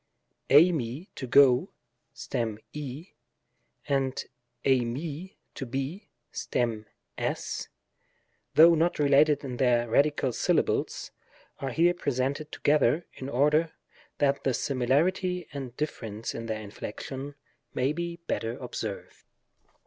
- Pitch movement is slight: No, average, 3.8 semitones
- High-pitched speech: No, medium, 140 Hz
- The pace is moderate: No, slow, 110 wpm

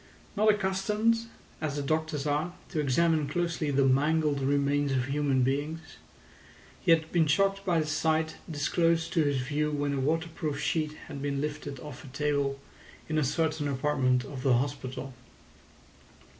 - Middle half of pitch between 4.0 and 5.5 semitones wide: No, narrow, 2.5 semitones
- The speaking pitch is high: No, medium, 150 Hz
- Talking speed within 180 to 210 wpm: No, average, 155 wpm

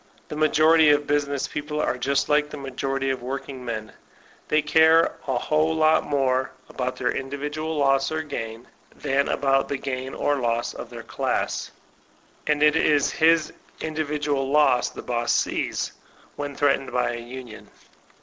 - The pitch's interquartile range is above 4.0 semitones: No, narrow, 2.4 semitones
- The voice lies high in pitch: No, medium, 140 Hz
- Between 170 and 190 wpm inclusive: No, average, 155 wpm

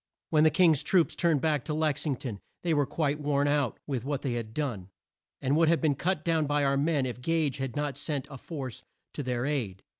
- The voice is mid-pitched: Yes, medium, 145 Hz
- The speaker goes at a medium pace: No, fast, 235 wpm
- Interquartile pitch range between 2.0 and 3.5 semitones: Yes, average, 2.8 semitones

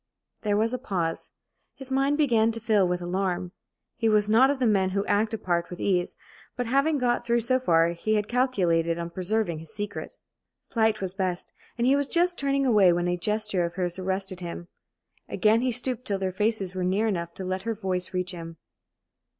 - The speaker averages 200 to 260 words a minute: Yes, fast, 205 wpm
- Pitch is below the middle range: No, high, 205 Hz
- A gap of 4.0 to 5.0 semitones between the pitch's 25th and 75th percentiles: Yes, average, 4.6 semitones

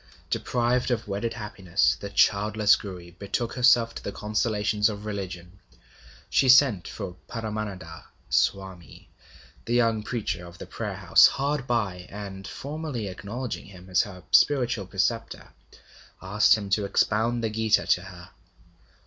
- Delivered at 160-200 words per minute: No, average, 140 wpm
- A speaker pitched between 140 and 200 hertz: No, low, 105 Hz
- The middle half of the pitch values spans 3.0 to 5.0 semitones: Yes, average, 3.4 semitones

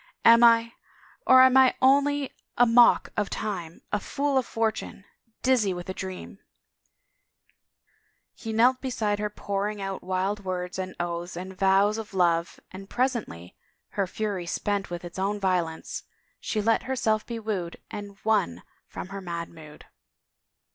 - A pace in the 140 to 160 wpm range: Yes, average, 155 wpm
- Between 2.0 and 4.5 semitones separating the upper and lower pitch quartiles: Yes, average, 3.7 semitones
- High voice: Yes, high, 200 Hz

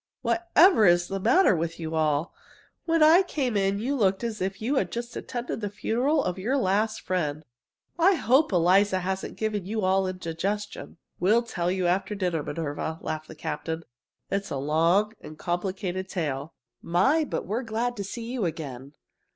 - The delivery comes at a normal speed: Yes, average, 170 wpm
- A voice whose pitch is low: No, high, 195 Hz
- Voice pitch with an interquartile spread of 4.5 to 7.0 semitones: Yes, wide, 5.4 semitones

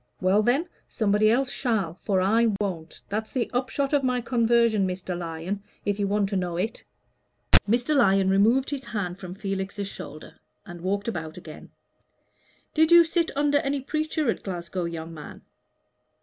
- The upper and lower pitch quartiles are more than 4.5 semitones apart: Yes, average, 5.3 semitones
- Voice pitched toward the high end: Yes, high, 205 Hz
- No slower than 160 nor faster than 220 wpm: Yes, average, 165 wpm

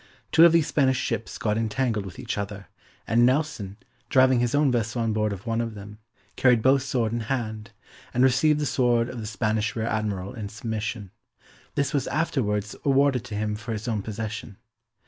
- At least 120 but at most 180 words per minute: No, average, 190 wpm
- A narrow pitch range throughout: No, average, 3.5 semitones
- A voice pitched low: Yes, low, 115 Hz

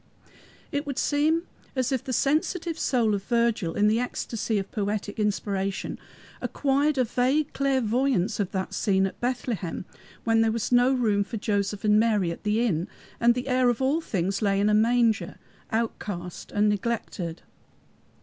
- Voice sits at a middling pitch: No, high, 225 Hz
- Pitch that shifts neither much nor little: Yes, average, 4.0 semitones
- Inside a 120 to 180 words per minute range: Yes, average, 165 wpm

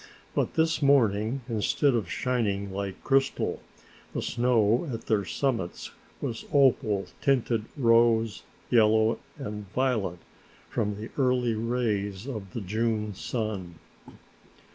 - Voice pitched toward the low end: Yes, low, 115 Hz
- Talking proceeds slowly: Yes, slow, 115 wpm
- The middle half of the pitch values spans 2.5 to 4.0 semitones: Yes, average, 3.4 semitones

